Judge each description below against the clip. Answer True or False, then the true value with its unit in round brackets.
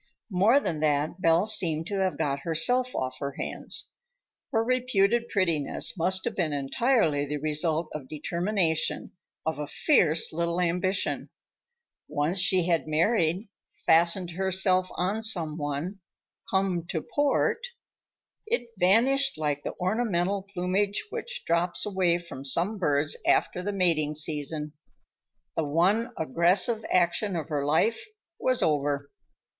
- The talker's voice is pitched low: False (175 Hz)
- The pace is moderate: False (130 wpm)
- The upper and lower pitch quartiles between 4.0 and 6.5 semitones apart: True (4.6 semitones)